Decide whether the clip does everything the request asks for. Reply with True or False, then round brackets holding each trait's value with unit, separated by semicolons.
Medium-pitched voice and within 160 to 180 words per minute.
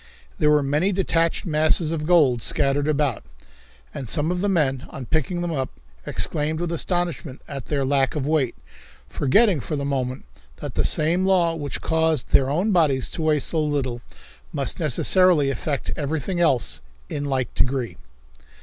True (150 Hz; 165 wpm)